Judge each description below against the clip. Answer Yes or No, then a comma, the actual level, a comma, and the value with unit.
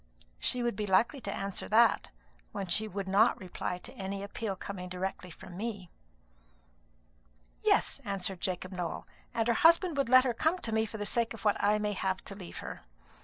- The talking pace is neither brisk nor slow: Yes, average, 195 wpm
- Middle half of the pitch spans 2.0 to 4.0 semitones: Yes, average, 3.3 semitones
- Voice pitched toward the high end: Yes, high, 200 Hz